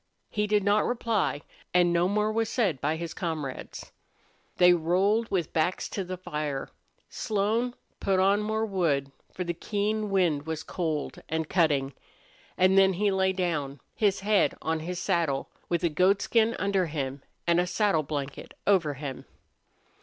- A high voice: No, medium, 180 Hz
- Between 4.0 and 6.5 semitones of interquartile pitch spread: Yes, average, 4.4 semitones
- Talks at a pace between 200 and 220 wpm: No, average, 160 wpm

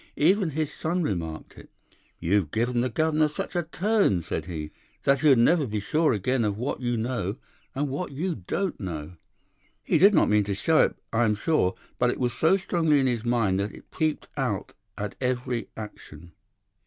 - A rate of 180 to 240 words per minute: Yes, average, 190 wpm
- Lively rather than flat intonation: Yes, wide, 7.3 semitones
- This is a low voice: Yes, low, 125 Hz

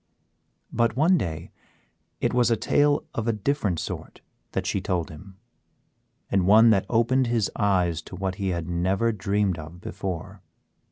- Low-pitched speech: Yes, low, 100 Hz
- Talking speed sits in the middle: Yes, average, 160 wpm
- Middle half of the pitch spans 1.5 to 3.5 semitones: No, average, 4.3 semitones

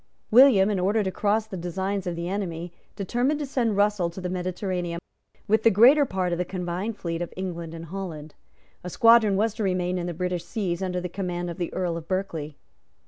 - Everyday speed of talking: No, fast, 210 wpm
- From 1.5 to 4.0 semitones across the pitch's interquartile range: Yes, average, 2.9 semitones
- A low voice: No, medium, 185 Hz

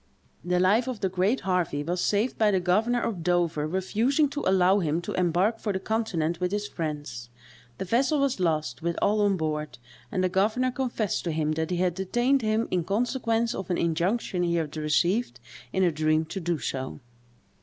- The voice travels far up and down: No, average, 4.9 semitones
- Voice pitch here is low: No, medium, 185 Hz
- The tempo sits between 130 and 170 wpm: No, average, 195 wpm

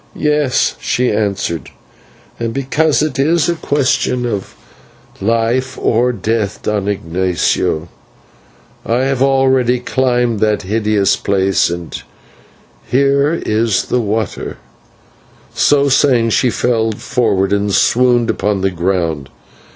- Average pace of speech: No, slow, 110 wpm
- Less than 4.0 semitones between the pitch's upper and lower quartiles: No, average, 4.5 semitones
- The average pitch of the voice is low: Yes, low, 115 Hz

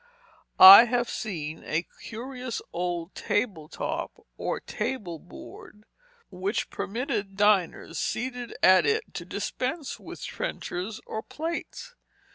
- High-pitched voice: Yes, high, 210 Hz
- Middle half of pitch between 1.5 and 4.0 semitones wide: No, wide, 5.6 semitones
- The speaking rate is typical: No, slow, 110 wpm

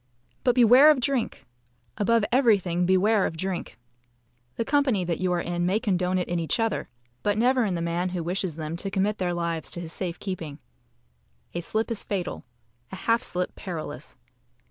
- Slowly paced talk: No, average, 185 wpm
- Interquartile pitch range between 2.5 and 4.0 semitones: No, average, 4.5 semitones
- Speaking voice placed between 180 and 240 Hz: Yes, medium, 185 Hz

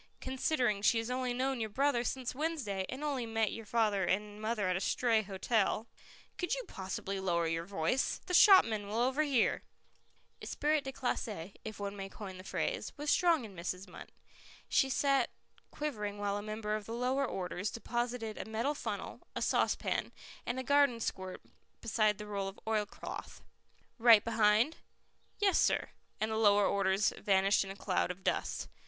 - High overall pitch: Yes, high, 220 Hz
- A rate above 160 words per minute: Yes, average, 175 wpm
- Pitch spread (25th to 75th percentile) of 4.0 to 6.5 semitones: Yes, average, 4.3 semitones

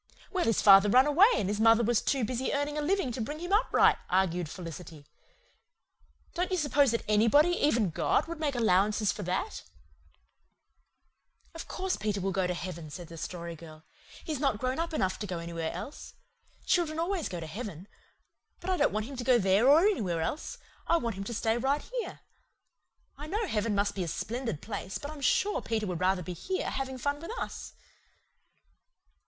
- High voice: Yes, high, 230 Hz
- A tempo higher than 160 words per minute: Yes, average, 195 wpm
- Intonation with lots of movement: Yes, wide, 7.8 semitones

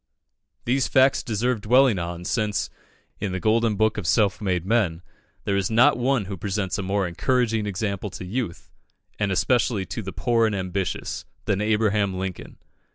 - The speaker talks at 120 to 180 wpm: Yes, average, 165 wpm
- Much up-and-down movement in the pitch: No, average, 3.3 semitones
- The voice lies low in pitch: Yes, low, 105 Hz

